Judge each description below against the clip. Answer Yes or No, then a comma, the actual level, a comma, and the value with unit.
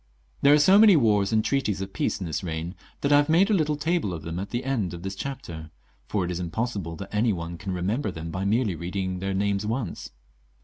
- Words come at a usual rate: No, fast, 250 wpm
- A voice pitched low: Yes, low, 100 Hz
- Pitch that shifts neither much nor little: No, wide, 7.0 semitones